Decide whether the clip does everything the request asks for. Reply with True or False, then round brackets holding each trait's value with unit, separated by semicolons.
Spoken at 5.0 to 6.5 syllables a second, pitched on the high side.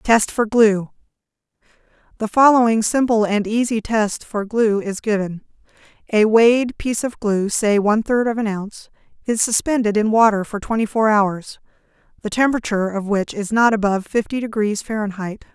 False (4.8 syllables/s; 215 Hz)